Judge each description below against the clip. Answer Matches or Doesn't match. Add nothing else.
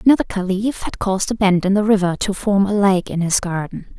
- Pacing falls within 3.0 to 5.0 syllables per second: Doesn't match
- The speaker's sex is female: Matches